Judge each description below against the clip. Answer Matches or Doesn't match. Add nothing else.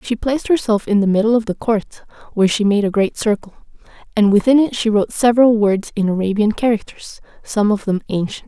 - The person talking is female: Matches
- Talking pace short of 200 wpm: Doesn't match